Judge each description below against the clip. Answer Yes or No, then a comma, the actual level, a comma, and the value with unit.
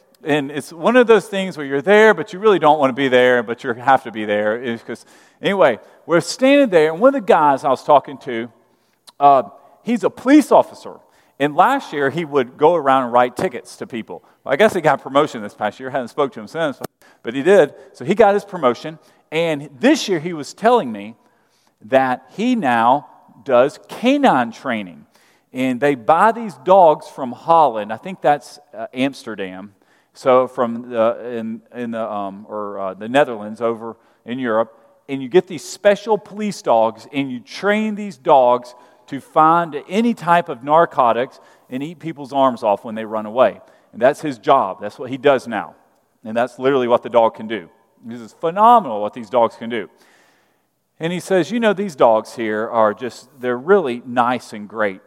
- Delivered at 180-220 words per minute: Yes, average, 200 wpm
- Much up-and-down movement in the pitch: Yes, wide, 7.7 semitones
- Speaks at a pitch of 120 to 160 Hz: Yes, medium, 140 Hz